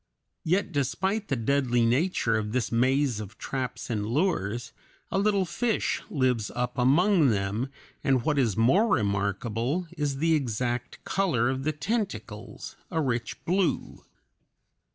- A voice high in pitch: No, low, 130 Hz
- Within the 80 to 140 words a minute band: Yes, slow, 135 wpm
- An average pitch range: No, wide, 5.9 semitones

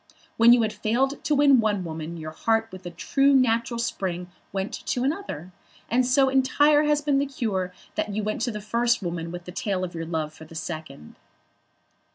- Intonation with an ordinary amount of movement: No, wide, 6.8 semitones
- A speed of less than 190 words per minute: No, average, 200 wpm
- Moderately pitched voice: No, high, 215 Hz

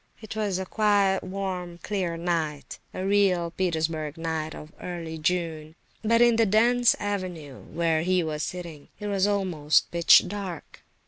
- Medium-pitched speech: Yes, medium, 180 Hz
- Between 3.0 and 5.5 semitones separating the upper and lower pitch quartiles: Yes, average, 3.8 semitones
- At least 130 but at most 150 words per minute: Yes, average, 145 wpm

